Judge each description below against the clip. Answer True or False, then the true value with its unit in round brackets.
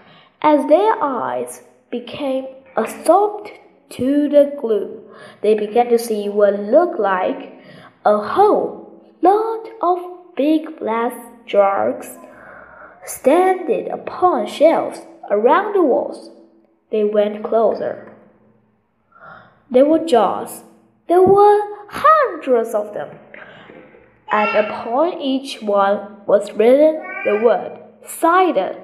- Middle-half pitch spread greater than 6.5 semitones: True (8.5 semitones)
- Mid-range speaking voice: False (270 Hz)